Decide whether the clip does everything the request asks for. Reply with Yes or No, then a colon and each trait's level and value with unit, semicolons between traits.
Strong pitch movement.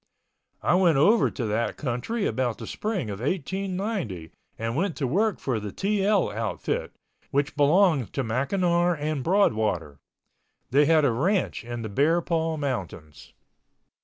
Yes: wide, 8.2 semitones